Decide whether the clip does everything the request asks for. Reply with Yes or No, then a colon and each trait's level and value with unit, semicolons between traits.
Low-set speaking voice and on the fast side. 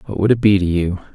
Yes: very low, 95 Hz; fast, 315 wpm